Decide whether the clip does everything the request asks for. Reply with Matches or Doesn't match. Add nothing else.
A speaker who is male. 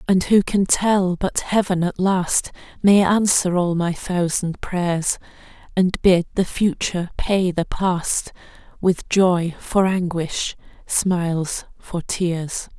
Doesn't match